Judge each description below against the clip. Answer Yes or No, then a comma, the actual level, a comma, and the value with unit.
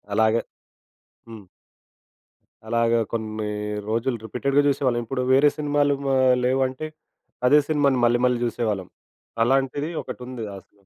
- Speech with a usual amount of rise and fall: Yes, average, 3.0 semitones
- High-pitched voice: No, low, 125 Hz